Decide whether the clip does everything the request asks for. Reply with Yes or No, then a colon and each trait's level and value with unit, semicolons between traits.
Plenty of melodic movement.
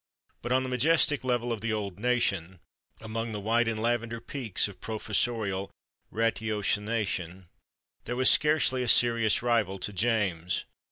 No: average, 2.9 semitones